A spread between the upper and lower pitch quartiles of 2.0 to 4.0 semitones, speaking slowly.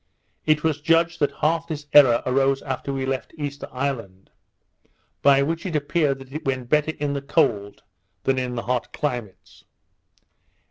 No: average, 2.8 semitones; average, 165 wpm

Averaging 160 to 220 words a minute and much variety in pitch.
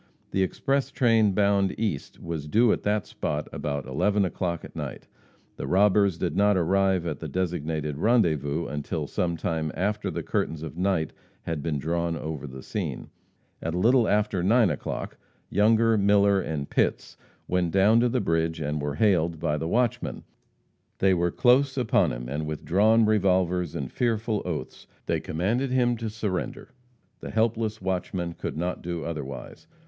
No: average, 165 wpm; average, 4.9 semitones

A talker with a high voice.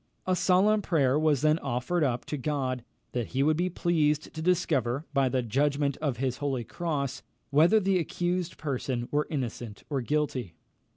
No: medium, 145 Hz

